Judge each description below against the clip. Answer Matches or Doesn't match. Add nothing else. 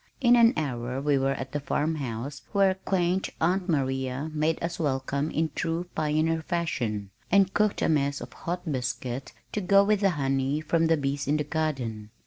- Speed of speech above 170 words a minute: Matches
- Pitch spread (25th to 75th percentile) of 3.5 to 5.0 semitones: Matches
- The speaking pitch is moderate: Matches